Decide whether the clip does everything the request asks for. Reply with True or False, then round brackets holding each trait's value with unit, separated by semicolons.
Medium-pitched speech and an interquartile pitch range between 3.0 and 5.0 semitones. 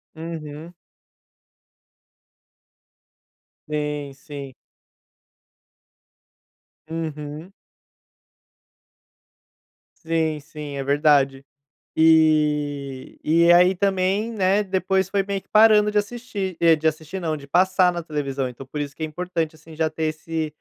True (160 Hz; 3.9 semitones)